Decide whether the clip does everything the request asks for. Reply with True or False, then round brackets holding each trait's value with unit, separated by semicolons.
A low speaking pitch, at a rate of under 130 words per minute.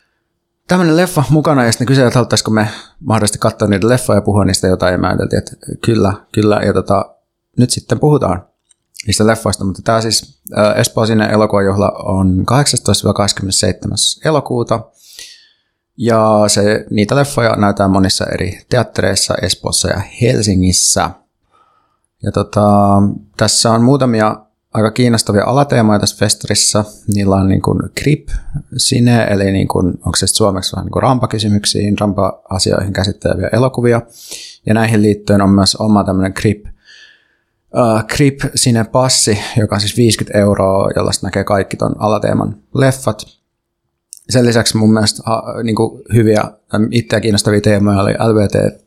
False (105 Hz; 140 wpm)